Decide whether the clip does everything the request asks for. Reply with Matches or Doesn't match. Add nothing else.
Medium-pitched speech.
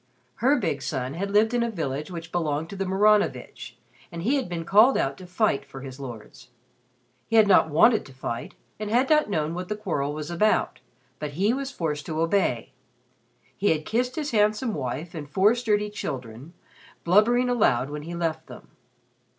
Matches